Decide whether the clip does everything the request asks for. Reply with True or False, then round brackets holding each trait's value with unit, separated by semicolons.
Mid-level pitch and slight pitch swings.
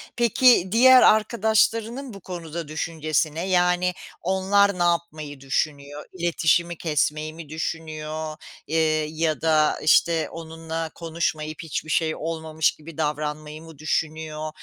True (160 Hz; 2.1 semitones)